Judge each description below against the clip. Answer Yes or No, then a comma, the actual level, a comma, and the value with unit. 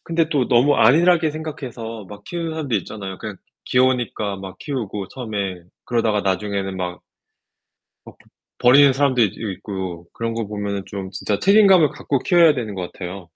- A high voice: No, low, 115 Hz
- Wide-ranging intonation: Yes, wide, 6.3 semitones